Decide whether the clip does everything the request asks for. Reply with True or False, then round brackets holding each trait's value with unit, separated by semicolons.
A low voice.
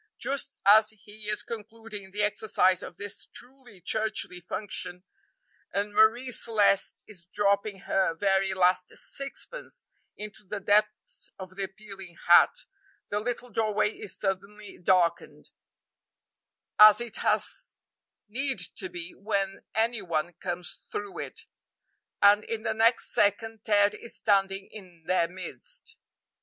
False (205 Hz)